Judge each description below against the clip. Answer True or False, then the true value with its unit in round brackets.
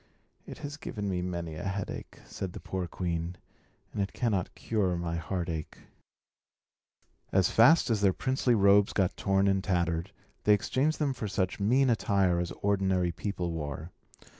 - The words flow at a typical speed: True (160 wpm)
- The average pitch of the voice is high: False (95 Hz)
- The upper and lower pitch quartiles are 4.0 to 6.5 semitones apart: False (3.0 semitones)